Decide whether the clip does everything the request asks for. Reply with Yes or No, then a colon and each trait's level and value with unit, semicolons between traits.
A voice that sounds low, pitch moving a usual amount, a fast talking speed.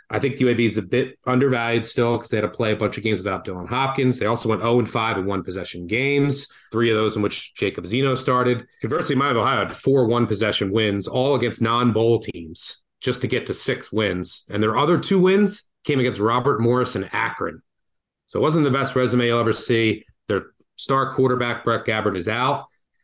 Yes: low, 120 Hz; average, 3.3 semitones; fast, 210 wpm